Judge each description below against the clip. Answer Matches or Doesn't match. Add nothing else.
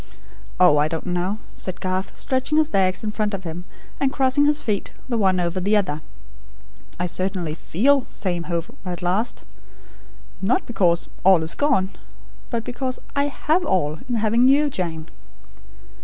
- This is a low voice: Doesn't match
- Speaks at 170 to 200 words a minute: Doesn't match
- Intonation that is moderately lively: Doesn't match